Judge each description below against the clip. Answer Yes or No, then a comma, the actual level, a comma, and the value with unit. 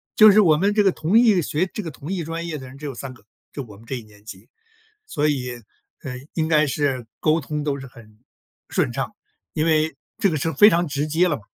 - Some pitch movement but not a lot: Yes, average, 4.2 semitones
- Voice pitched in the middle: Yes, medium, 150 Hz